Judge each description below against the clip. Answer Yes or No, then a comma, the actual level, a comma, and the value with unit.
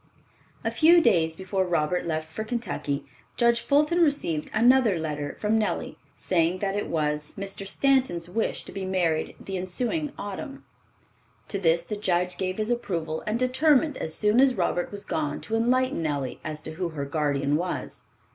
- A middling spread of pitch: No, wide, 6.6 semitones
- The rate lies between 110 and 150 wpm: No, average, 170 wpm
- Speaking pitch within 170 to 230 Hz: Yes, high, 190 Hz